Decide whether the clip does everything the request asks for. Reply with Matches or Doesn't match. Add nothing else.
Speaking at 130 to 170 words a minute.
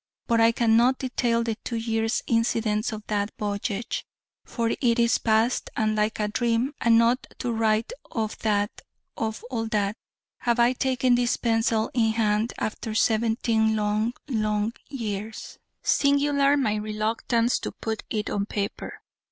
Matches